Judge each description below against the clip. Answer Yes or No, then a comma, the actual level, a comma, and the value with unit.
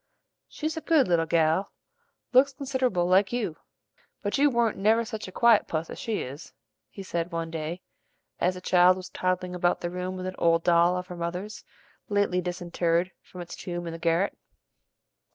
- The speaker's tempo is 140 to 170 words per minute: No, average, 185 wpm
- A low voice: No, medium, 180 Hz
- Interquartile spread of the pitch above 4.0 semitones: No, average, 3.3 semitones